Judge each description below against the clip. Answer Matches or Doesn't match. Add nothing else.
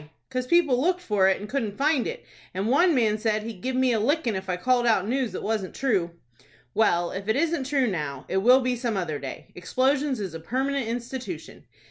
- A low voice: Doesn't match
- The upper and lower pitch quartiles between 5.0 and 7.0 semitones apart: Matches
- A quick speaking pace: Matches